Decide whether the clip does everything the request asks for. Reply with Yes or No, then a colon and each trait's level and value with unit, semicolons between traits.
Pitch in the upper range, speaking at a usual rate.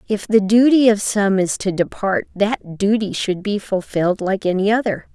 Yes: high, 205 Hz; average, 185 wpm